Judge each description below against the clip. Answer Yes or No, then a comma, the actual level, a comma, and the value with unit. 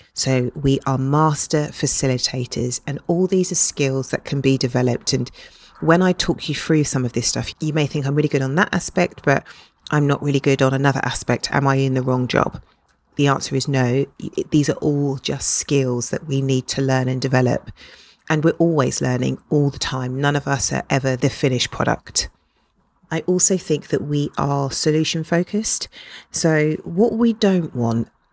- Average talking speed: Yes, average, 195 wpm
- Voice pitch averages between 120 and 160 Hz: Yes, medium, 140 Hz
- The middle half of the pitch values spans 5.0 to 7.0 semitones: No, average, 3.1 semitones